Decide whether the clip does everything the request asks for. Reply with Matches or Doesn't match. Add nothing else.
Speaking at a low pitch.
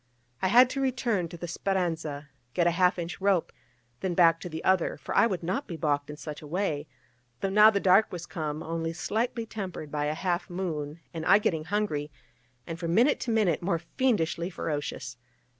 Doesn't match